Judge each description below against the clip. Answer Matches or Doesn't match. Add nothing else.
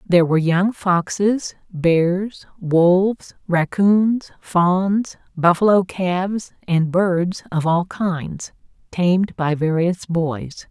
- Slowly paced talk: Matches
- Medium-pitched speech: Matches